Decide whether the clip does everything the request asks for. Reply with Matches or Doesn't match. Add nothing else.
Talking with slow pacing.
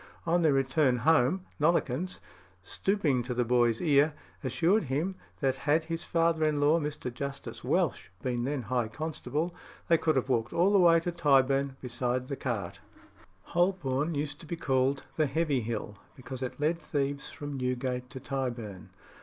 Doesn't match